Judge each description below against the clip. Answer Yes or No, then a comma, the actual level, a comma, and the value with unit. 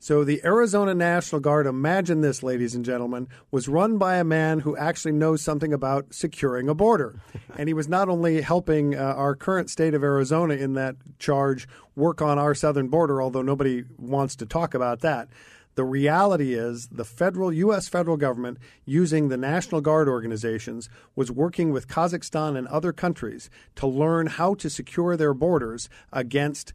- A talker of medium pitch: Yes, medium, 150 Hz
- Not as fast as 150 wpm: No, average, 175 wpm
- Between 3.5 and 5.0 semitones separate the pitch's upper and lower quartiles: Yes, average, 4.0 semitones